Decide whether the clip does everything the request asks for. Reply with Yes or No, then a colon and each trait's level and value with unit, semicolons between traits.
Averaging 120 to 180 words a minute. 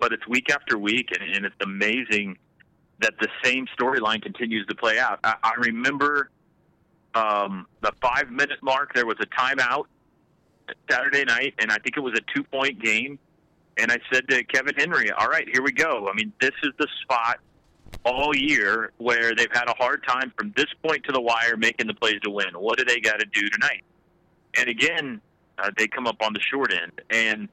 No: fast, 205 wpm